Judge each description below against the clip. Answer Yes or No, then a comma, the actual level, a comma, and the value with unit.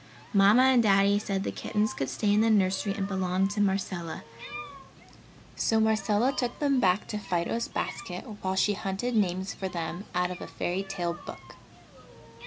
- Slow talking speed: No, average, 170 wpm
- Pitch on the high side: Yes, high, 195 Hz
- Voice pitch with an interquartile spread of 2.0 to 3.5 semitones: Yes, narrow, 2.5 semitones